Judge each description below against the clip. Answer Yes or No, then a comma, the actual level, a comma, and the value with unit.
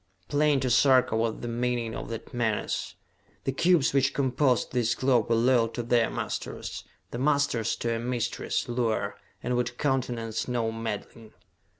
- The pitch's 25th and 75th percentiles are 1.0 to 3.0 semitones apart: Yes, narrow, 2.5 semitones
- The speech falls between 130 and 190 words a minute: Yes, average, 160 wpm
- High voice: No, low, 120 Hz